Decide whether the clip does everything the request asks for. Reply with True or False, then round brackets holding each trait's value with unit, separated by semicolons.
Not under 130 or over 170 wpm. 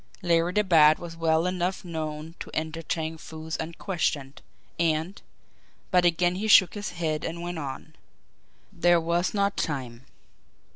True (145 wpm)